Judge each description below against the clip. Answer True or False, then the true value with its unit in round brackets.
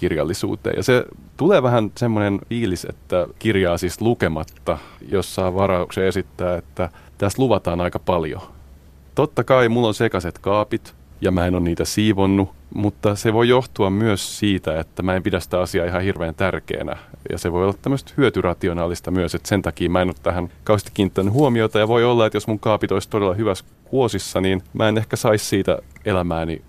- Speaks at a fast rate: True (180 wpm)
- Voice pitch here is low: True (95 Hz)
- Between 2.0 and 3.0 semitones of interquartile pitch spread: False (3.6 semitones)